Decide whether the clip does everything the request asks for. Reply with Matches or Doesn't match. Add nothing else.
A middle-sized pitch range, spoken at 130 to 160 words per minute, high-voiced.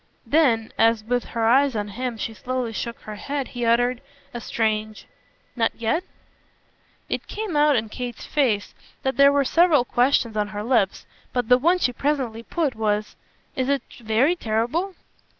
Doesn't match